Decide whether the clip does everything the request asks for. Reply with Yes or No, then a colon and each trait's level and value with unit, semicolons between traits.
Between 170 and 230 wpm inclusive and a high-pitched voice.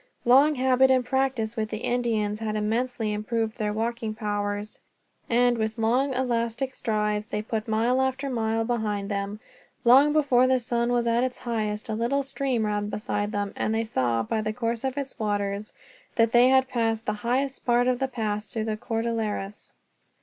Yes: average, 180 wpm; high, 230 Hz